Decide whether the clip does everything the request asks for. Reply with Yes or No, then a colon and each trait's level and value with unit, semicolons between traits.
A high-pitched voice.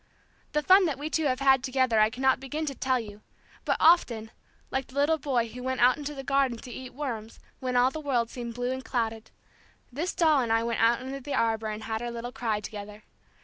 Yes: very high, 255 Hz